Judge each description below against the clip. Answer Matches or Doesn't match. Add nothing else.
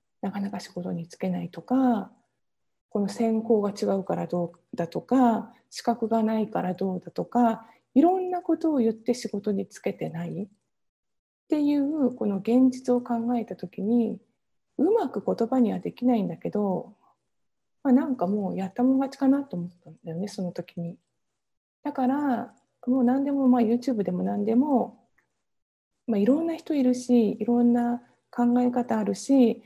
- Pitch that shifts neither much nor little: Matches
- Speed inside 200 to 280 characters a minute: Doesn't match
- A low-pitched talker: Doesn't match